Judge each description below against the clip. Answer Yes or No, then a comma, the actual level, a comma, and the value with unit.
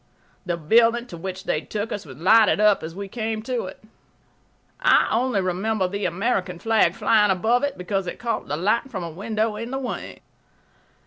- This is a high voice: Yes, high, 210 Hz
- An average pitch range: Yes, average, 3.8 semitones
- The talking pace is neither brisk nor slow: Yes, average, 190 wpm